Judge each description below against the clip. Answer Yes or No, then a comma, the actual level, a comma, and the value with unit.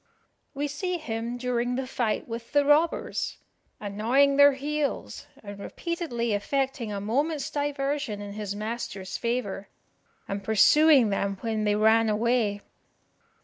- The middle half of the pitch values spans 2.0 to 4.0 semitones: No, average, 5.1 semitones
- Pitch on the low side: No, high, 235 Hz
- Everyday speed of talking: No, slow, 130 wpm